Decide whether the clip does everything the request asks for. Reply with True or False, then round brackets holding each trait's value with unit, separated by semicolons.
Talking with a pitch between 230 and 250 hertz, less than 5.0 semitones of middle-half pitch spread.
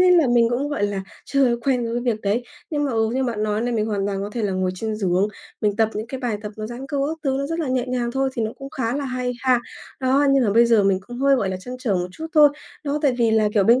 True (240 Hz; 3.9 semitones)